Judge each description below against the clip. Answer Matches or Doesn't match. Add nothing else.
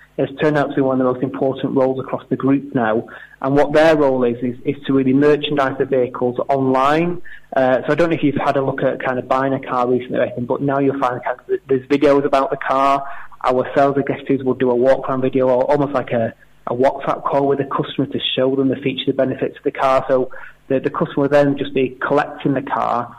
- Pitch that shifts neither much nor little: Doesn't match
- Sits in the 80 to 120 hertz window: Doesn't match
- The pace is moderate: Doesn't match